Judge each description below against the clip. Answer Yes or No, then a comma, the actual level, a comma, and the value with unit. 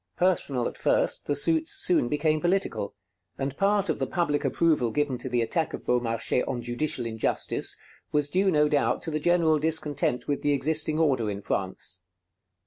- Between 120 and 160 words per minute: No, average, 175 wpm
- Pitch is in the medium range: Yes, medium, 150 Hz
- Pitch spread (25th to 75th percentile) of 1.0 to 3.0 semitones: No, average, 4.5 semitones